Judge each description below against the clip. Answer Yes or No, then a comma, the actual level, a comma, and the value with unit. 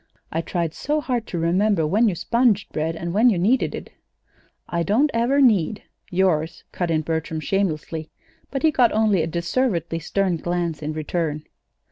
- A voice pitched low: No, medium, 175 Hz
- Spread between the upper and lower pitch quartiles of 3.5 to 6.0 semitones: Yes, average, 5.2 semitones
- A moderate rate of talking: Yes, average, 170 wpm